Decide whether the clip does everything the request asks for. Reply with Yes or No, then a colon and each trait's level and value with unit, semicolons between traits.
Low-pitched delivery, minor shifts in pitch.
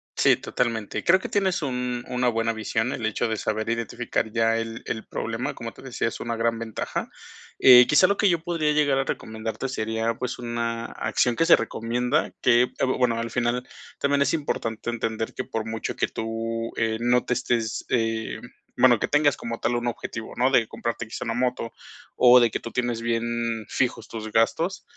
Yes: low, 115 Hz; narrow, 1.8 semitones